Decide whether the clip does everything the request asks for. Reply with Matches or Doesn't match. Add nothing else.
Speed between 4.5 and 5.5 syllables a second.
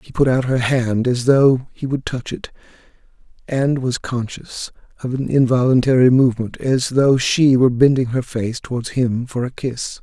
Matches